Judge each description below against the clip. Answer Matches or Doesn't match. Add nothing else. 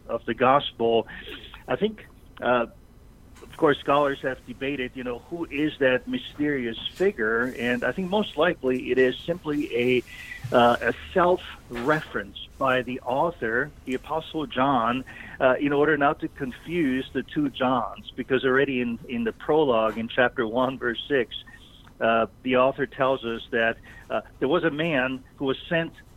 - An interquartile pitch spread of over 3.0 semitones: Matches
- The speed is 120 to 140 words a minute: Doesn't match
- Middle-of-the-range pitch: Doesn't match